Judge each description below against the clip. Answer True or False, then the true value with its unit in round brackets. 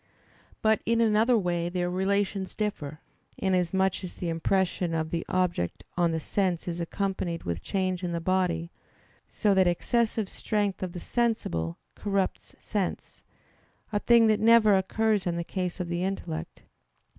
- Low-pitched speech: False (185 Hz)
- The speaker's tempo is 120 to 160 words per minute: True (155 wpm)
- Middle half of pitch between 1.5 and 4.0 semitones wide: True (3.1 semitones)